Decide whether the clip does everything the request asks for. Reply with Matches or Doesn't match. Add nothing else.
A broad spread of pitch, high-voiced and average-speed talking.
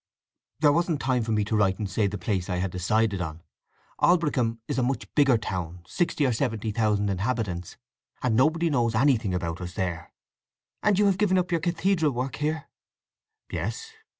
Doesn't match